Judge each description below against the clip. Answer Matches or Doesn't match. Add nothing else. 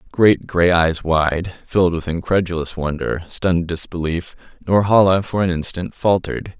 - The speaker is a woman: Doesn't match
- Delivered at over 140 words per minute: Doesn't match